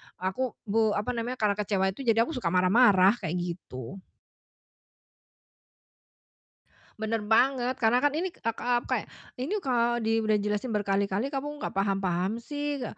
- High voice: Yes, high, 220 Hz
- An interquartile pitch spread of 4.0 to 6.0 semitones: Yes, average, 4.4 semitones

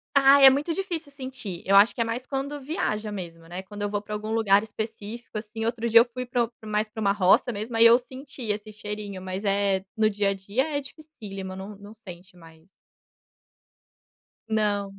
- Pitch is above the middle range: Yes, high, 215 Hz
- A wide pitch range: No, average, 3.7 semitones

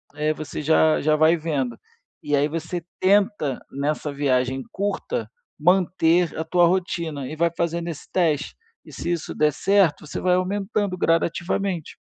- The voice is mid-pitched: Yes, medium, 165 Hz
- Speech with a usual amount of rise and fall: Yes, average, 3.3 semitones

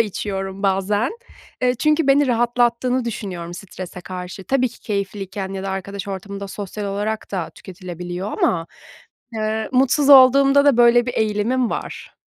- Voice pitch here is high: Yes, high, 210 Hz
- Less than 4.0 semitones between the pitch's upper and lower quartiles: No, average, 4.3 semitones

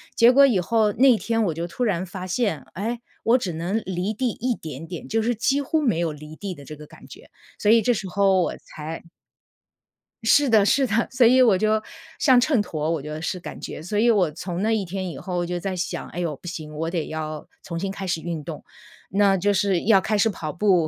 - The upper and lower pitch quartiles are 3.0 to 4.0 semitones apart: No, average, 4.9 semitones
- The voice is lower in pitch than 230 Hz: Yes, high, 195 Hz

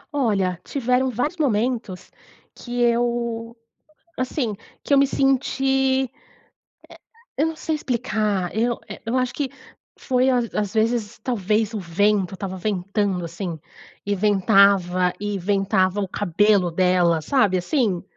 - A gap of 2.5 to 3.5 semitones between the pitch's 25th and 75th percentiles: No, average, 4.8 semitones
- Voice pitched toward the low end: No, high, 215 Hz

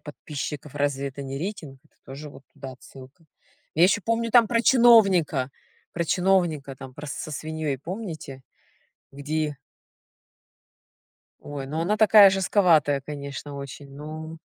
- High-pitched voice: No, medium, 150 Hz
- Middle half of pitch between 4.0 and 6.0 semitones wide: Yes, average, 4.7 semitones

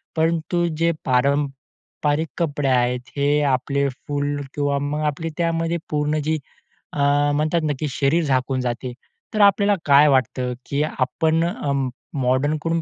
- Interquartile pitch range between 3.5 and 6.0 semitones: No, average, 2.8 semitones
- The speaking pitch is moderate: Yes, medium, 145 Hz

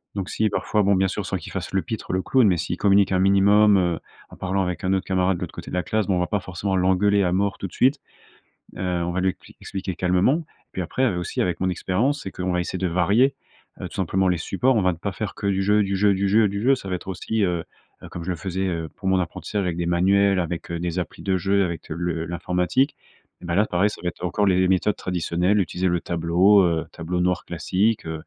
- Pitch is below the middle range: Yes, very low, 95 Hz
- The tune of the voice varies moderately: No, narrow, 2.2 semitones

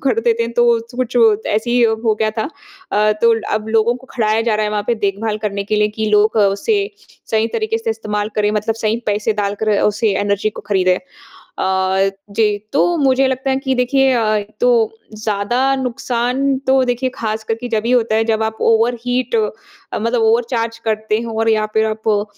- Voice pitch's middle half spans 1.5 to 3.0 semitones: Yes, narrow, 2.6 semitones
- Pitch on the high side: Yes, high, 225 Hz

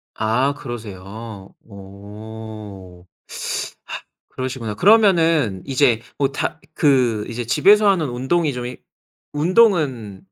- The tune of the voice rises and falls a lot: Yes, wide, 5.7 semitones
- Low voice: Yes, low, 120 Hz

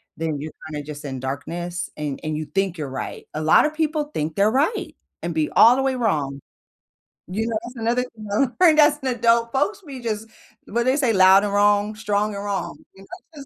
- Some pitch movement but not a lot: No, wide, 7.7 semitones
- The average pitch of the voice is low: No, high, 205 Hz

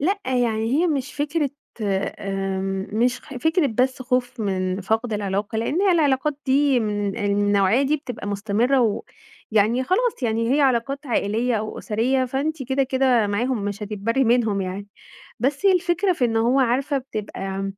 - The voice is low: No, high, 245 Hz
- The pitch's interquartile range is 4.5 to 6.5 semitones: Yes, average, 4.8 semitones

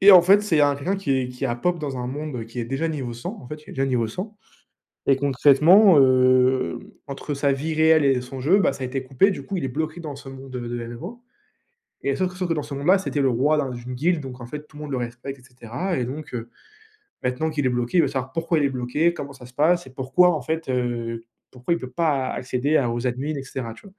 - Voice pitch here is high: No, low, 135 Hz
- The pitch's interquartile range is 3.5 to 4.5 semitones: Yes, average, 4.0 semitones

